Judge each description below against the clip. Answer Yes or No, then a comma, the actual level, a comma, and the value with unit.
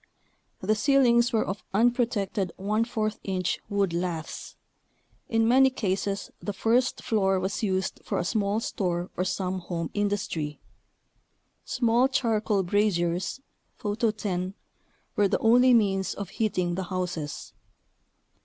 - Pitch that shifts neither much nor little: Yes, average, 3.5 semitones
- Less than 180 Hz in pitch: No, high, 200 Hz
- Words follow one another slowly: Yes, slow, 125 wpm